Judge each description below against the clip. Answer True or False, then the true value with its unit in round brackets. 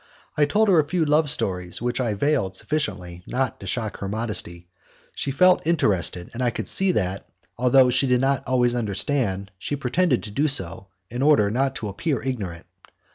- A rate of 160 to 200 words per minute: True (185 wpm)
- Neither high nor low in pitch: False (125 Hz)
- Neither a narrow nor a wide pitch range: False (6.4 semitones)